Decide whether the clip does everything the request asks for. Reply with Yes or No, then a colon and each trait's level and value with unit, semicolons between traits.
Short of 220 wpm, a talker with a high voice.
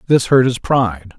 No: average, 200 wpm; low, 120 Hz